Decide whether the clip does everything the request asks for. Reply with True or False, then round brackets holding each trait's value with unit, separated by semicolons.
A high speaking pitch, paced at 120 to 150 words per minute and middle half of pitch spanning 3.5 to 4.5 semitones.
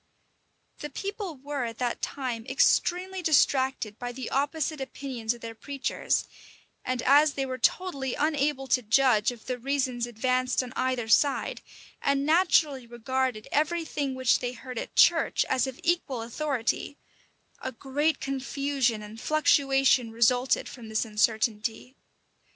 False (260 Hz; 140 wpm; 3.1 semitones)